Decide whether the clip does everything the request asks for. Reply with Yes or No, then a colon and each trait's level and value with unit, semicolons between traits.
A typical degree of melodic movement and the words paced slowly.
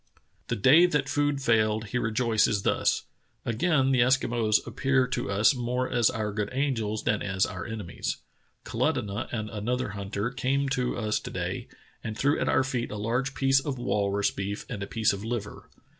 No: average, 3.8 semitones; average, 180 wpm